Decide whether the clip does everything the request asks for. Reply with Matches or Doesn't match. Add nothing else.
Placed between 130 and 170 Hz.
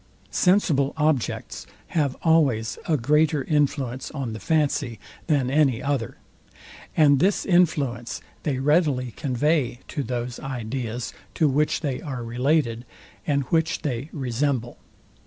Matches